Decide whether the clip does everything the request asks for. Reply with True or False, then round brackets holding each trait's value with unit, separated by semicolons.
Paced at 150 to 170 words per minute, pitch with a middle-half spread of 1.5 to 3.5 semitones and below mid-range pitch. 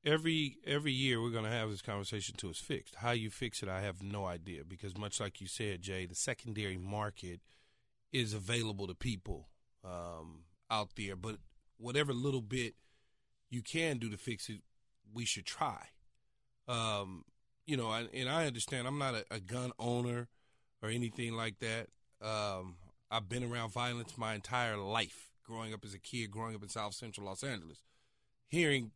False (180 wpm; 3.1 semitones; 115 Hz)